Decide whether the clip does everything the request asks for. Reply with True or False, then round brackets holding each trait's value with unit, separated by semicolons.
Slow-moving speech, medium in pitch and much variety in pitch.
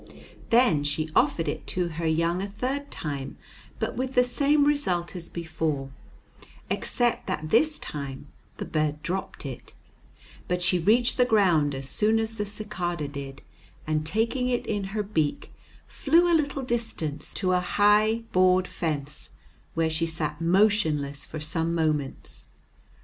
False (150 wpm; 180 Hz; 6.2 semitones)